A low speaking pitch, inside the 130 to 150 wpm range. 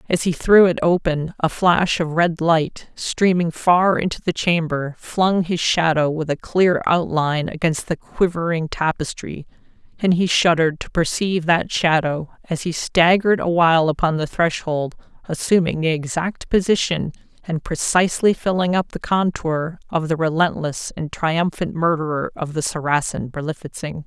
No: medium, 165 Hz; average, 145 wpm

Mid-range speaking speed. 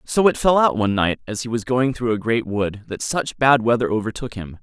No: fast, 260 wpm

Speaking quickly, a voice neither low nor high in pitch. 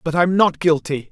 Yes: fast, 215 wpm; medium, 165 Hz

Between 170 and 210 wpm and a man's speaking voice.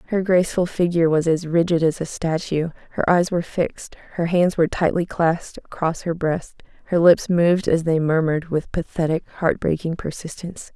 No: average, 180 wpm; female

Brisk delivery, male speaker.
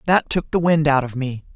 Yes: fast, 270 wpm; male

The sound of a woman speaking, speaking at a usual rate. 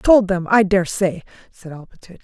Yes: female; average, 190 wpm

